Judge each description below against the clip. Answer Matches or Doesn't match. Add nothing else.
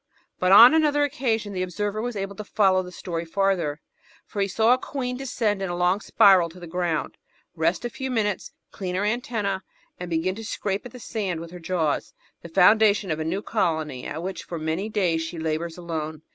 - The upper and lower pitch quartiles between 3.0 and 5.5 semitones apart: Matches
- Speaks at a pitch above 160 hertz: Matches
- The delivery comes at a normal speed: Doesn't match